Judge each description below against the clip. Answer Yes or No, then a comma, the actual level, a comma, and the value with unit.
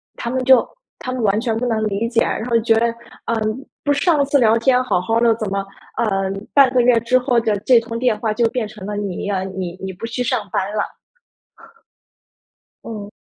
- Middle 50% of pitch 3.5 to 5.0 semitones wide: No, average, 3.1 semitones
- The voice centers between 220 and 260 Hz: Yes, high, 230 Hz